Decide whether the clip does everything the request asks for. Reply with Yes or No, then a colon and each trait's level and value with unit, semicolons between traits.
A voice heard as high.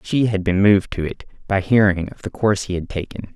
No: low, 100 Hz